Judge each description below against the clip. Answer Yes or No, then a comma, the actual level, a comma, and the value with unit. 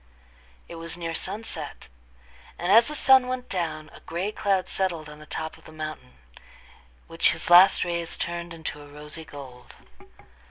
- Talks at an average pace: Yes, average, 165 wpm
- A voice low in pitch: No, medium, 170 Hz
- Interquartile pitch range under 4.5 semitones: Yes, average, 3.6 semitones